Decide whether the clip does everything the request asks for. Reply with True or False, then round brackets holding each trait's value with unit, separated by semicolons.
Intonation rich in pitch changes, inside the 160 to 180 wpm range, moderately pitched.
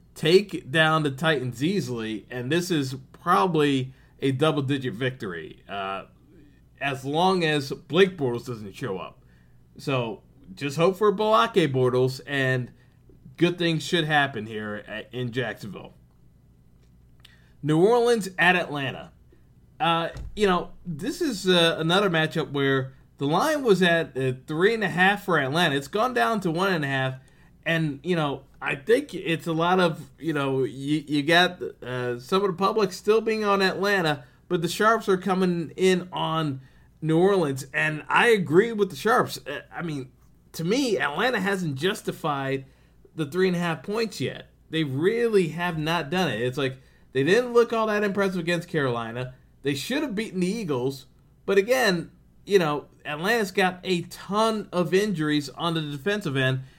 True (5.9 semitones; 165 wpm; 160 Hz)